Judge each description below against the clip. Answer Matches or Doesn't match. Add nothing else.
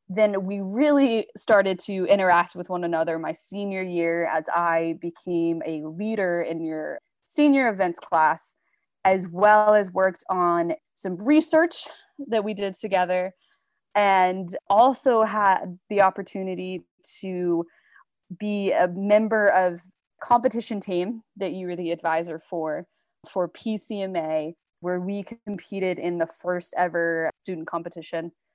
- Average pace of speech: Doesn't match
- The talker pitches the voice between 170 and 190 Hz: Matches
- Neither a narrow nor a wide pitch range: Matches